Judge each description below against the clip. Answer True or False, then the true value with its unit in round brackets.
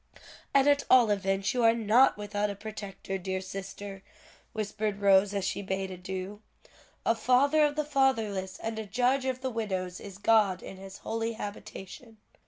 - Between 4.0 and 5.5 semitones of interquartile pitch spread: False (3.2 semitones)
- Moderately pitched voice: False (210 Hz)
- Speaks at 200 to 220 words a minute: False (170 wpm)